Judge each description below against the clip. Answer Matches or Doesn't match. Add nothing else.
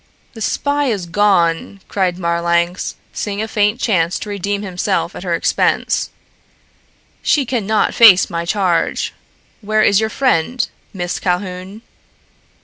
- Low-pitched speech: Doesn't match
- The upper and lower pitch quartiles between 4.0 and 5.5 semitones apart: Doesn't match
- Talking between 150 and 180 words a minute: Doesn't match